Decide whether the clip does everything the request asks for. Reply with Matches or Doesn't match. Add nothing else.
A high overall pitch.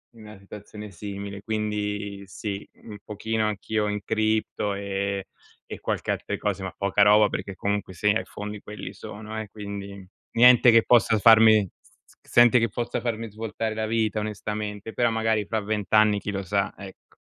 Doesn't match